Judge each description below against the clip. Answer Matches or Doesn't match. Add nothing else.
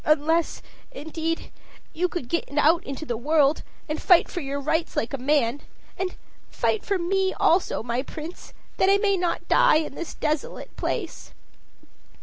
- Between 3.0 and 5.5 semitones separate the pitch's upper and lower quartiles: Matches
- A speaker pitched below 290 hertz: Doesn't match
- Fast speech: Doesn't match